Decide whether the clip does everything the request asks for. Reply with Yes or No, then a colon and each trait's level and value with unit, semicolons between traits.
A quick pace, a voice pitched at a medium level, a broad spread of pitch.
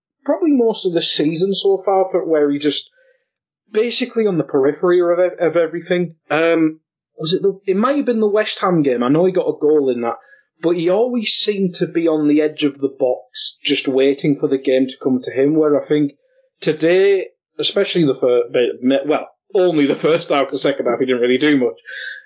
Yes: fast, 210 wpm; medium, 180 Hz; wide, 8.2 semitones